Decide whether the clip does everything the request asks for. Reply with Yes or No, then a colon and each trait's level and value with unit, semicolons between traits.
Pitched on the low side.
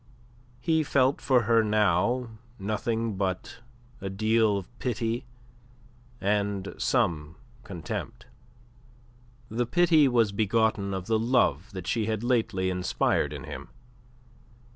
Yes: low, 110 Hz